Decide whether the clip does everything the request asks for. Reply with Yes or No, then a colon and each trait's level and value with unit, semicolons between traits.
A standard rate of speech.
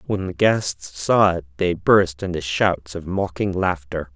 Yes: average, 175 wpm